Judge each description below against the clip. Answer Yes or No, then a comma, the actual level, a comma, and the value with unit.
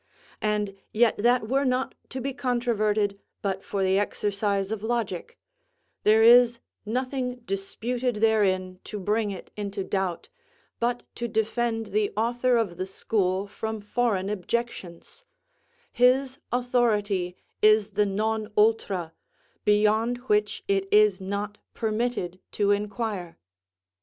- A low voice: No, high, 215 Hz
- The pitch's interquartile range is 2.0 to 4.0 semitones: Yes, average, 3.1 semitones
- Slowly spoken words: Yes, slow, 120 wpm